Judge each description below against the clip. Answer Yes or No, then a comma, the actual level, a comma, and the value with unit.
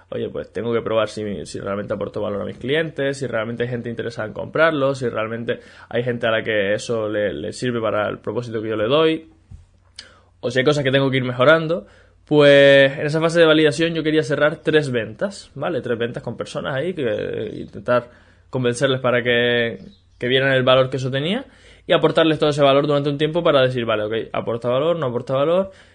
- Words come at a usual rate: No, fast, 215 wpm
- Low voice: Yes, low, 130 Hz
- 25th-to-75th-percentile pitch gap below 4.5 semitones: No, average, 5.0 semitones